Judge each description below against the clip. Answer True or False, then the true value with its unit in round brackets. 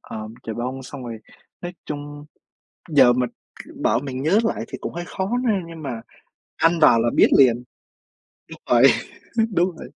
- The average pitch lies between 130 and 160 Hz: True (135 Hz)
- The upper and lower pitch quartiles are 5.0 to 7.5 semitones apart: True (5.3 semitones)